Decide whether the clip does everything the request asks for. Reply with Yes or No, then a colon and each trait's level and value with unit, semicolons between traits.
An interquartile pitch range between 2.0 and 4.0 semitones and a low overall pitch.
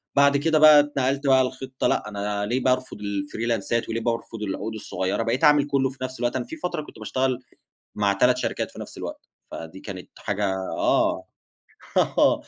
No: average, 4.5 semitones; low, 125 Hz